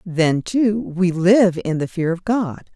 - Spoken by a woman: Yes, female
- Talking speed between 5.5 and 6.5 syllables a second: No, 3.5 syllables/s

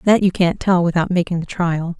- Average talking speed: No, fast, 240 wpm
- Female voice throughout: Yes, female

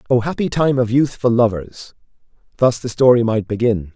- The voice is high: No, low, 120 Hz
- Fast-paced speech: No, average, 165 wpm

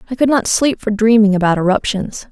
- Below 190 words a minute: No, fast, 205 wpm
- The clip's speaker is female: Yes, female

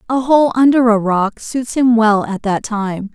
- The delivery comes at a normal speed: No, fast, 210 wpm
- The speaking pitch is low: No, high, 230 Hz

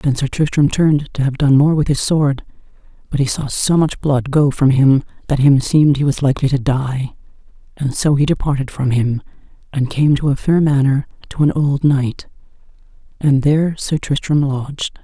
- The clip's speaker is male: No, female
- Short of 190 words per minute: No, average, 195 wpm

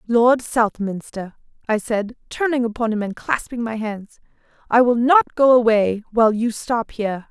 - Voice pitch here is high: Yes, high, 230 Hz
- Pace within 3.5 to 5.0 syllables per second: Yes, 4.6 syllables/s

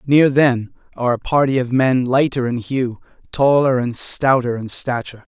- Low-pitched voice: Yes, low, 130 Hz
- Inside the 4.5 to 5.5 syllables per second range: Yes, 4.8 syllables/s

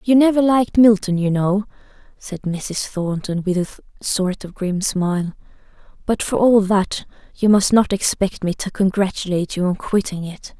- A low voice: No, high, 195 Hz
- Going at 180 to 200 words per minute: No, average, 170 wpm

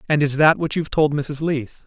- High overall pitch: No, medium, 150 Hz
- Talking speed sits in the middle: No, fast, 260 wpm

